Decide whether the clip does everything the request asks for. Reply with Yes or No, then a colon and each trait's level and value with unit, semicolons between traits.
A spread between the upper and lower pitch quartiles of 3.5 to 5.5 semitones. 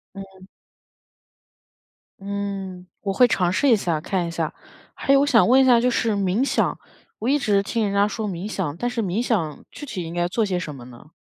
Yes: average, 4.6 semitones